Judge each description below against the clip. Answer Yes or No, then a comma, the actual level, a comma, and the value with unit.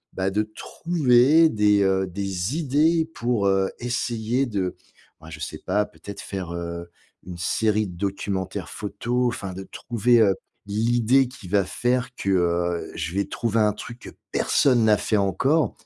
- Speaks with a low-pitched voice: Yes, low, 105 Hz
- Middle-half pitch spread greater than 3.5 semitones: Yes, average, 4.2 semitones